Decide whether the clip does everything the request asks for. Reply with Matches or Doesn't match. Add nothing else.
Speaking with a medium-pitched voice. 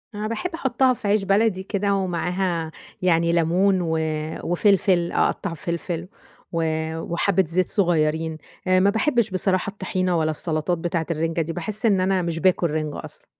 Matches